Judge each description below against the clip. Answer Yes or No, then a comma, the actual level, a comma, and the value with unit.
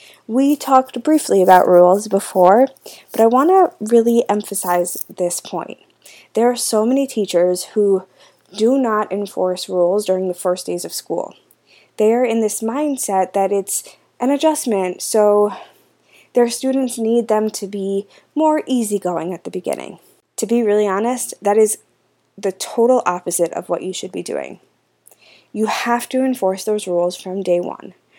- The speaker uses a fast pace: No, average, 160 wpm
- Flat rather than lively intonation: No, average, 4.5 semitones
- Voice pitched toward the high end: Yes, high, 210 Hz